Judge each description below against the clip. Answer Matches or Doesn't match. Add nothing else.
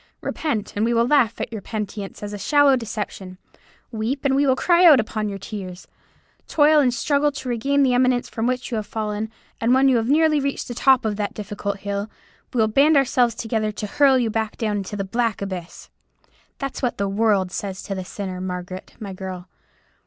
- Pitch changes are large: Doesn't match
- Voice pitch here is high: Matches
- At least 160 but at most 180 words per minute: Doesn't match